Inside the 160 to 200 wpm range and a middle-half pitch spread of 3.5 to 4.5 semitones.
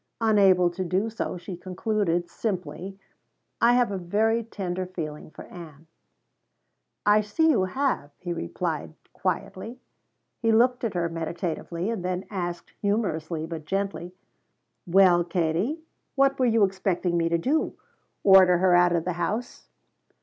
No: average, 140 wpm; average, 3.8 semitones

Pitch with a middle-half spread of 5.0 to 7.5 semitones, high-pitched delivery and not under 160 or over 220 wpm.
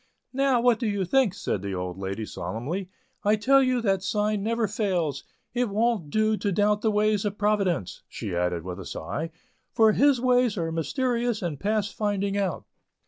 Yes: average, 5.3 semitones; high, 205 Hz; average, 185 wpm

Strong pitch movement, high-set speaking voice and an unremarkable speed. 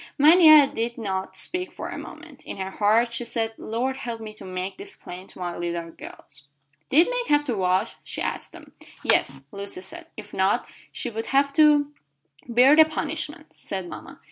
Yes: wide, 7.5 semitones; high, 230 Hz; average, 195 wpm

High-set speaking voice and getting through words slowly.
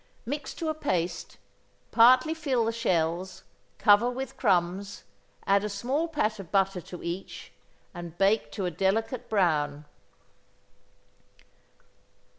Yes: high, 200 Hz; slow, 120 wpm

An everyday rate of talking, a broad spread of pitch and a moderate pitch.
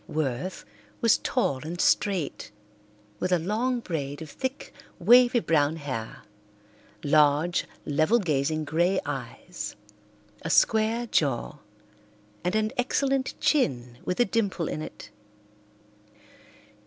No: slow, 110 wpm; wide, 7.4 semitones; medium, 175 Hz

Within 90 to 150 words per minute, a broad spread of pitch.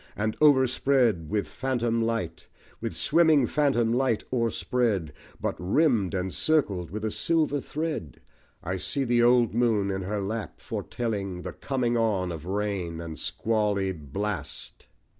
No: average, 140 wpm; average, 4.7 semitones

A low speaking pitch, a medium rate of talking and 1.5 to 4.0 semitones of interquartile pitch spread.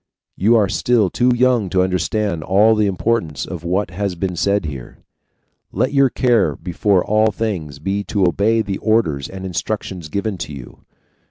Yes: low, 100 Hz; average, 165 wpm; average, 3.6 semitones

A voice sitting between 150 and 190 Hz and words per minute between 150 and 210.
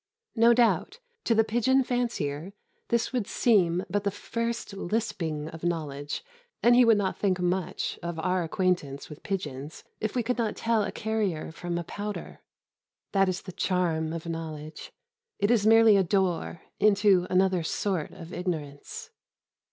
Yes: medium, 185 Hz; average, 160 wpm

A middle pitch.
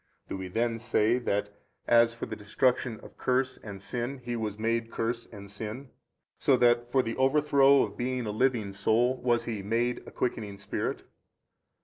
No: low, 115 Hz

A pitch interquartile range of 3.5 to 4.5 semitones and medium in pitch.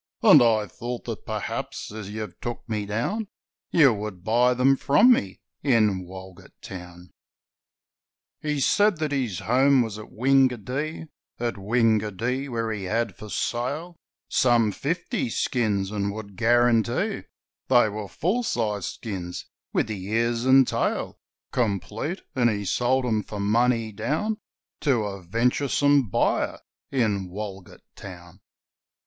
No: average, 4.1 semitones; low, 115 Hz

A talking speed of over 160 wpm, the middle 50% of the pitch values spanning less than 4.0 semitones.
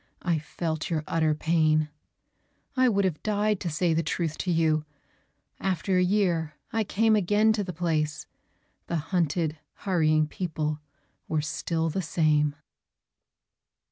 No: average, 140 wpm; average, 3.4 semitones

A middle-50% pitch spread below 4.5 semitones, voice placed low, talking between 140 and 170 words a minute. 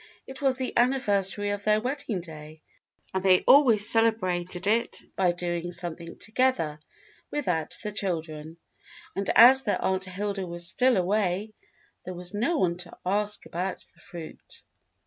No: average, 4.0 semitones; high, 195 Hz; average, 145 wpm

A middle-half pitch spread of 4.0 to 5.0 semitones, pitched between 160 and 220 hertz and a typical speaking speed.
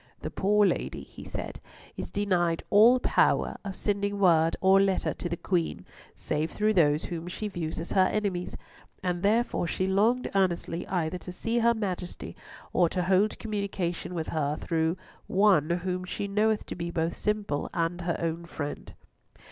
No: average, 3.2 semitones; medium, 185 Hz; average, 170 wpm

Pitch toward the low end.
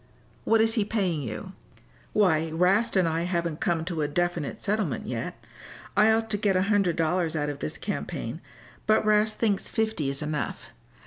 No: medium, 180 Hz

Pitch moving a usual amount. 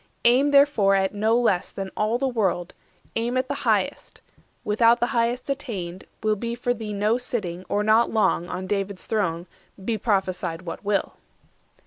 Yes: average, 3.8 semitones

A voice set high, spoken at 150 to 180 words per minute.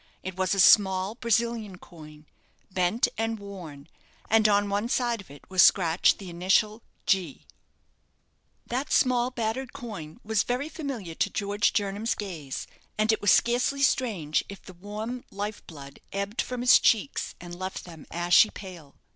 Yes: high, 200 Hz; average, 155 wpm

